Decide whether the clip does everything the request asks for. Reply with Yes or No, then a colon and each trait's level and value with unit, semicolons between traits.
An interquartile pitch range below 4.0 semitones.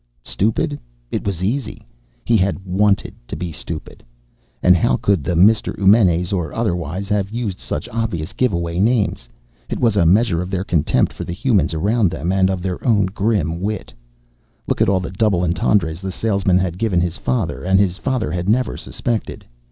Yes: average, 3.4 semitones